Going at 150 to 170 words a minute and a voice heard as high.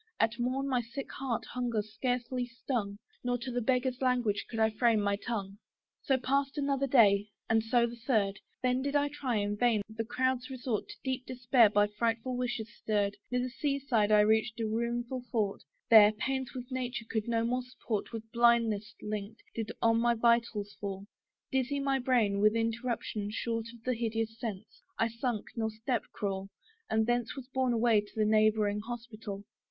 No: average, 180 wpm; high, 230 Hz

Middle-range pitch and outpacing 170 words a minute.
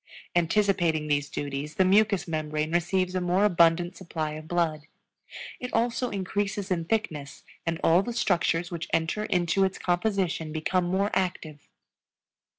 No: medium, 175 Hz; average, 145 wpm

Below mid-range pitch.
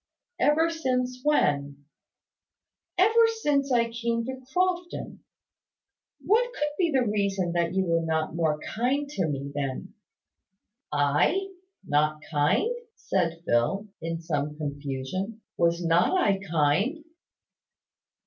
No: high, 190 Hz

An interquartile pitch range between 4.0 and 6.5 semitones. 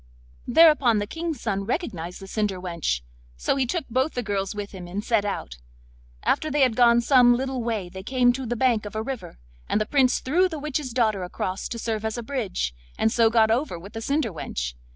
Yes: average, 4.5 semitones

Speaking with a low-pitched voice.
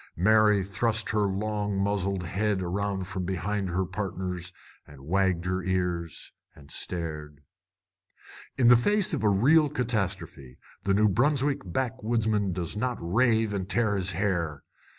Yes: low, 100 Hz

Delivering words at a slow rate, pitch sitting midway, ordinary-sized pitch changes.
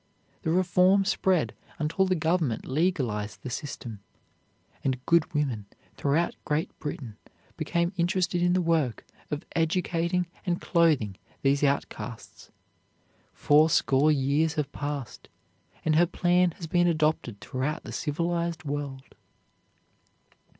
Yes: slow, 115 wpm; medium, 155 Hz; average, 3.8 semitones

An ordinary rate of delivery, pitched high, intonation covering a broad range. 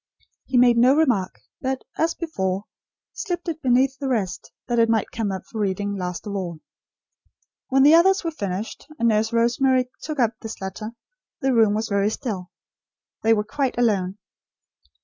No: average, 170 wpm; high, 230 Hz; average, 4.8 semitones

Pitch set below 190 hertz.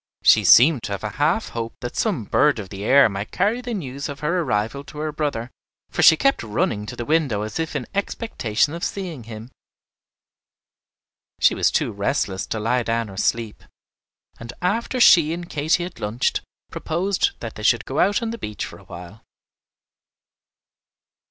Yes: medium, 140 Hz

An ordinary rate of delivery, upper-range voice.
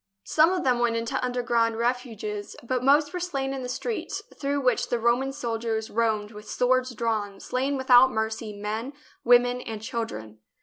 Yes: average, 170 wpm; high, 240 Hz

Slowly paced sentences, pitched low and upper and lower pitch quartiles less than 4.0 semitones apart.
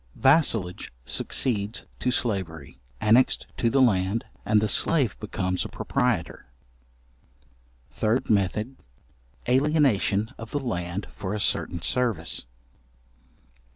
No: slow, 105 wpm; low, 110 Hz; average, 5.1 semitones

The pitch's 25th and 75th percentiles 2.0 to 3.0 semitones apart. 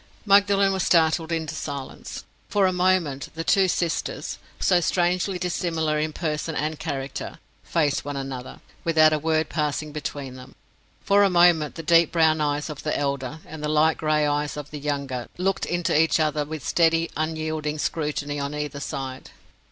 Yes: narrow, 2.4 semitones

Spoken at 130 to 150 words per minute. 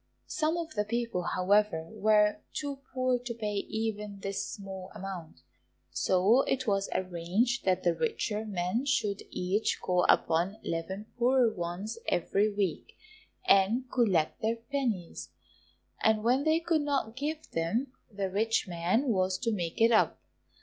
Yes: average, 145 wpm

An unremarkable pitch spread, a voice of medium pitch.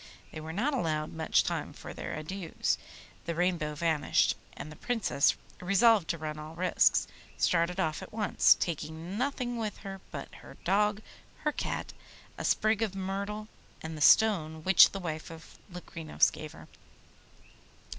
Yes: average, 4.7 semitones; medium, 180 Hz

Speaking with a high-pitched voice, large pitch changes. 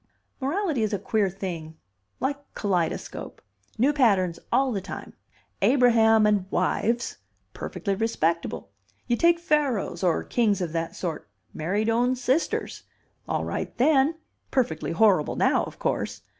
Yes: high, 220 Hz; wide, 5.8 semitones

